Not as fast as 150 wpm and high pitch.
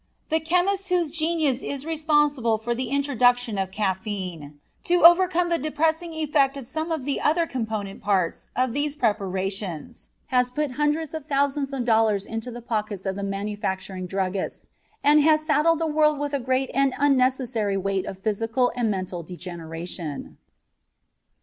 No: average, 155 wpm; very high, 255 Hz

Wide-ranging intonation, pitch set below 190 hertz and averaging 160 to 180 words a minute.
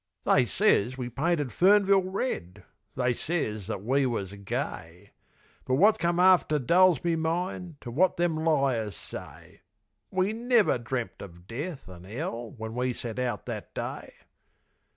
No: wide, 7.6 semitones; low, 135 Hz; average, 150 wpm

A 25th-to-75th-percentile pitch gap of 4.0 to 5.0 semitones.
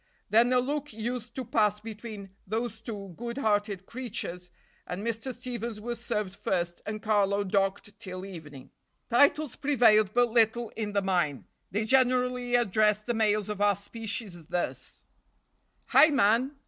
No: average, 3.1 semitones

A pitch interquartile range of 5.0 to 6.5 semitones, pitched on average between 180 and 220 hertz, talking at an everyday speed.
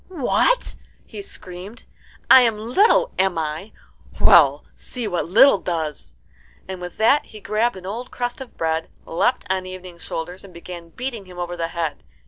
Yes: wide, 5.5 semitones; high, 190 Hz; average, 165 wpm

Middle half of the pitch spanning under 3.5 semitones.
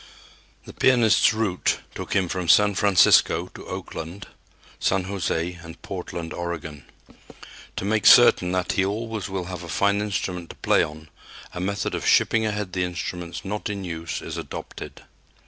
Yes: average, 2.9 semitones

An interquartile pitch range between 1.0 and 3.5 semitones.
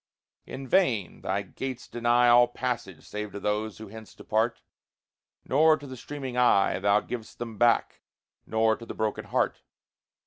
Yes: average, 2.8 semitones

